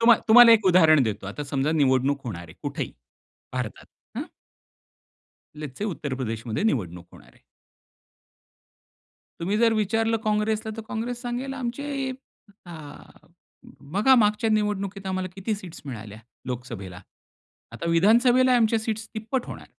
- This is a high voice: Yes, high, 205 Hz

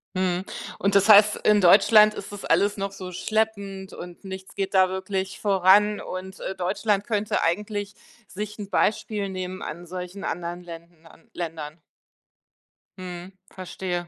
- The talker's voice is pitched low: No, high, 190 Hz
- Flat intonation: Yes, narrow, 2.3 semitones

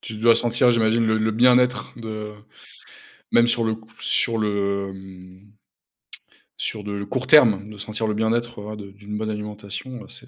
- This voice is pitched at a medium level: No, low, 110 Hz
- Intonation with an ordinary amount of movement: No, narrow, 2.2 semitones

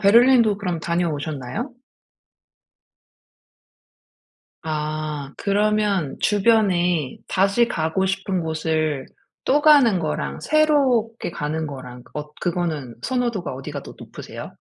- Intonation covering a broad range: Yes, wide, 5.9 semitones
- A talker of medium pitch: Yes, medium, 175 Hz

